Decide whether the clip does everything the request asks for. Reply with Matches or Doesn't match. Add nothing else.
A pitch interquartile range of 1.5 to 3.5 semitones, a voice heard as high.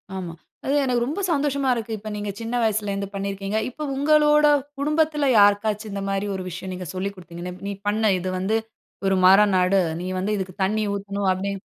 Doesn't match